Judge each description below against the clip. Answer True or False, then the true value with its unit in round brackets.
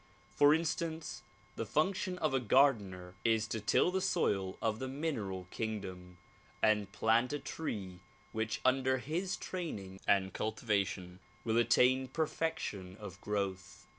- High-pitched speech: False (110 Hz)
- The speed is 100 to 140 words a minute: True (135 wpm)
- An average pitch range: False (6.8 semitones)